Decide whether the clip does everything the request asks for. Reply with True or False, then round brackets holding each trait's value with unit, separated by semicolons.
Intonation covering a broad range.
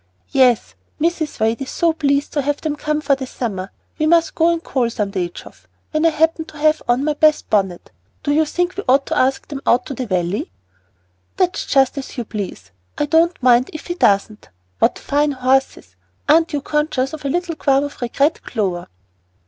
False (4.4 semitones)